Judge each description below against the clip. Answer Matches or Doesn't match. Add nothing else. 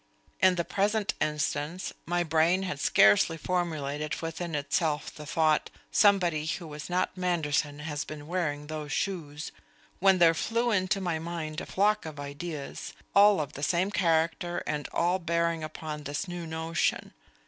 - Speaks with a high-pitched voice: Doesn't match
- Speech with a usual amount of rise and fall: Matches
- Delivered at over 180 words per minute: Doesn't match